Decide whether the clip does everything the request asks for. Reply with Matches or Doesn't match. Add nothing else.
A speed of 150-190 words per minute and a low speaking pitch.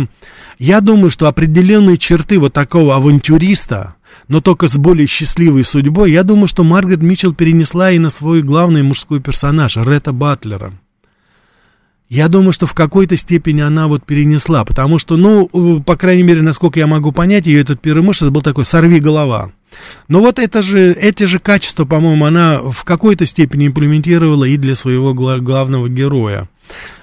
Doesn't match